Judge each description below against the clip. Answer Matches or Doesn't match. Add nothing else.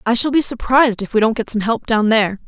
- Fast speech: Matches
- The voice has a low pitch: Doesn't match